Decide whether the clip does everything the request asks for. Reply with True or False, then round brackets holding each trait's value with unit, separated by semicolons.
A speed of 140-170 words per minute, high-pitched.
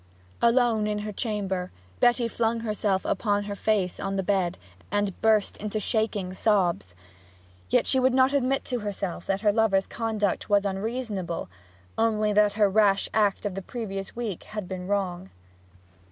True (160 wpm; 205 Hz)